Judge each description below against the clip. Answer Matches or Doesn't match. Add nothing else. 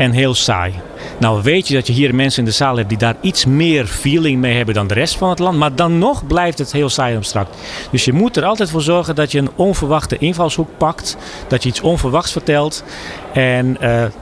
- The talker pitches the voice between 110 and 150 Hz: Matches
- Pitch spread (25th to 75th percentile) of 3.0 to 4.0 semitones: Doesn't match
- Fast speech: Matches